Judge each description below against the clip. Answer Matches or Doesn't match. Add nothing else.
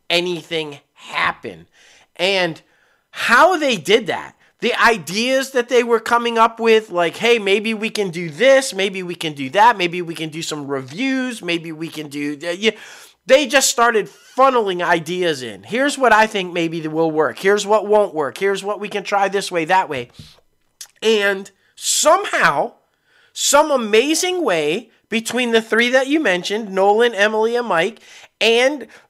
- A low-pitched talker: Doesn't match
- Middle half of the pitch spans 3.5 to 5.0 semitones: Doesn't match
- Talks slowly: Doesn't match